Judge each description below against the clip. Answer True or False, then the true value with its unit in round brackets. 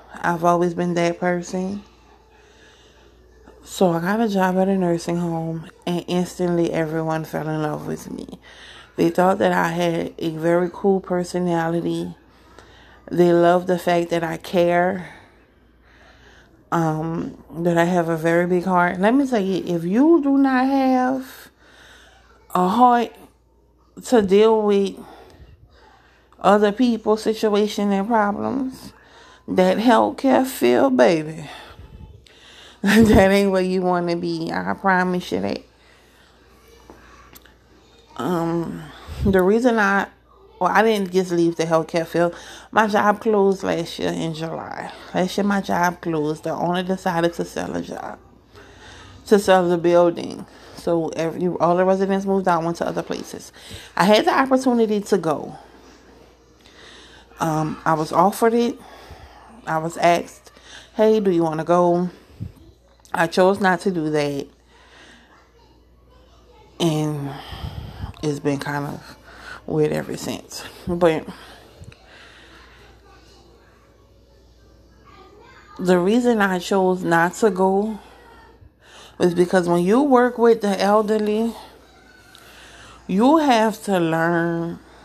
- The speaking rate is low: True (125 wpm)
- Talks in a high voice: False (180 Hz)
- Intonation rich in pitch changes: False (3.8 semitones)